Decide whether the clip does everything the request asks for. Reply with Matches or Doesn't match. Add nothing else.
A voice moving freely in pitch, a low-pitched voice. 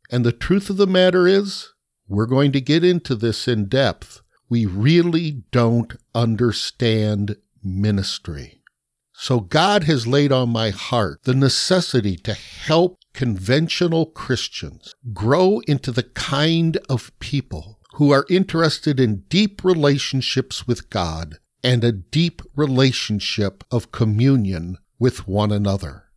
Matches